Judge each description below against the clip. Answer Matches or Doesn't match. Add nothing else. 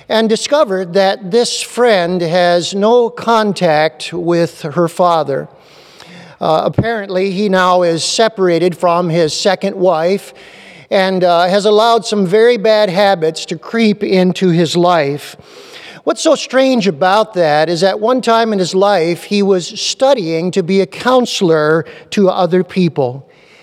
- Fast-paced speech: Doesn't match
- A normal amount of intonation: Matches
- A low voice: Doesn't match